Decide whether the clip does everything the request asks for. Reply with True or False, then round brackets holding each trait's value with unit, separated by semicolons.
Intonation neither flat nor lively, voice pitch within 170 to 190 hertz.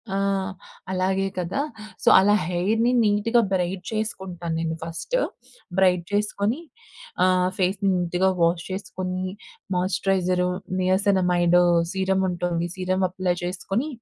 False (1.7 semitones; 185 Hz)